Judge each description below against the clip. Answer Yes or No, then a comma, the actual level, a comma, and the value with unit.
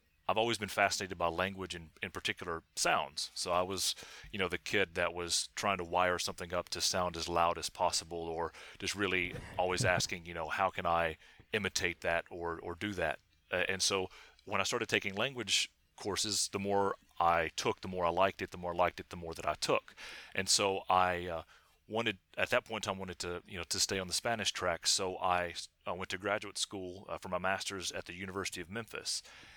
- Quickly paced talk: Yes, fast, 225 wpm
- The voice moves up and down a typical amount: No, narrow, 2.2 semitones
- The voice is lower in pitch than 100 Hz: Yes, very low, 90 Hz